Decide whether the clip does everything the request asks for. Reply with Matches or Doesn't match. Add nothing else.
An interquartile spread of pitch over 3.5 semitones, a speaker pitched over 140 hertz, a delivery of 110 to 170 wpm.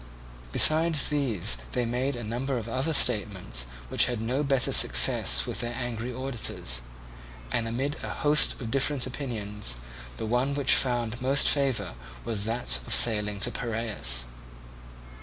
Doesn't match